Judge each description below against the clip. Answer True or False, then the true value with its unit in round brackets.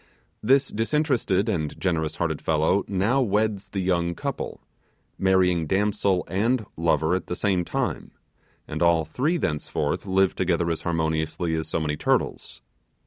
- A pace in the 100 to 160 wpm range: True (140 wpm)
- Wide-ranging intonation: False (4.0 semitones)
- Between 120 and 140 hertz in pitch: False (90 Hz)